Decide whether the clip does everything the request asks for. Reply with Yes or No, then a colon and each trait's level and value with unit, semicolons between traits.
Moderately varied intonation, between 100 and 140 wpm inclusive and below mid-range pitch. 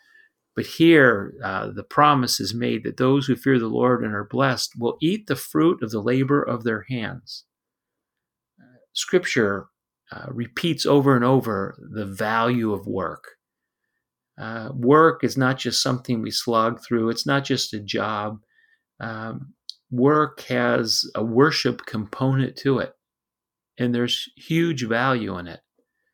No: average, 3.5 semitones; average, 150 wpm; low, 120 Hz